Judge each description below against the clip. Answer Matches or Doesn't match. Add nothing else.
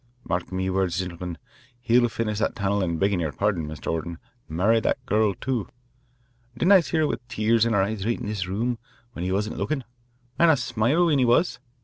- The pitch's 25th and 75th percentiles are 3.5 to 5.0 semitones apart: Matches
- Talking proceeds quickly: Matches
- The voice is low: Matches